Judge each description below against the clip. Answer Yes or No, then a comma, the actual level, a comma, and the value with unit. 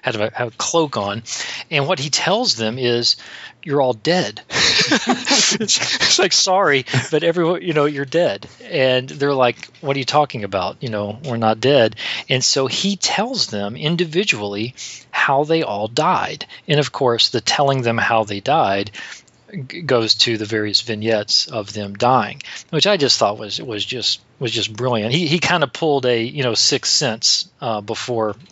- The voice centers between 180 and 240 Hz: No, low, 130 Hz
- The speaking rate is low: No, average, 185 wpm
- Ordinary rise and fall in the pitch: No, wide, 5.9 semitones